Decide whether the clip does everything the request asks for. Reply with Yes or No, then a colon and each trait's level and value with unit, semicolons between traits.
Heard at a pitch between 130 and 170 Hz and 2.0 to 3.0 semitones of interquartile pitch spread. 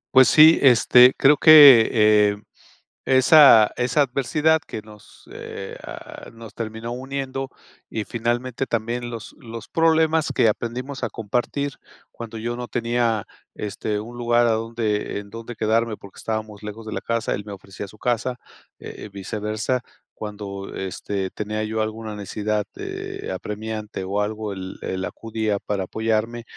No: low, 115 Hz; narrow, 2.6 semitones